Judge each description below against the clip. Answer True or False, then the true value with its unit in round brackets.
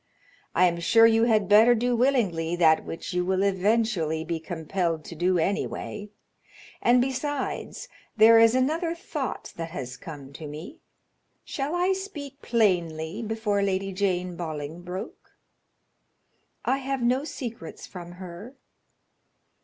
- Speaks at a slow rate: True (130 wpm)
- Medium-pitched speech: False (200 Hz)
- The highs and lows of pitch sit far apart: True (6.1 semitones)